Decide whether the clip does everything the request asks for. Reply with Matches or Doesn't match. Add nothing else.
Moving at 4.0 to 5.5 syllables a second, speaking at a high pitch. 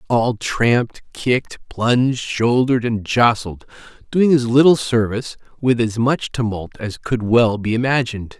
Doesn't match